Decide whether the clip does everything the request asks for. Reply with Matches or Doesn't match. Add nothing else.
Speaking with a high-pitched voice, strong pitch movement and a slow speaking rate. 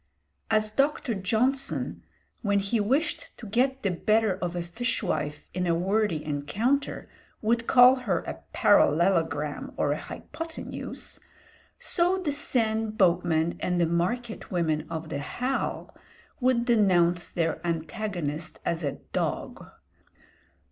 Matches